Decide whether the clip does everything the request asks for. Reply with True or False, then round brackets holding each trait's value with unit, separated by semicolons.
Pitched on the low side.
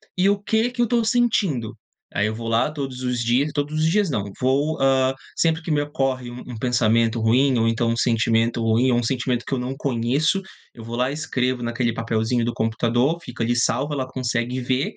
True (125 Hz)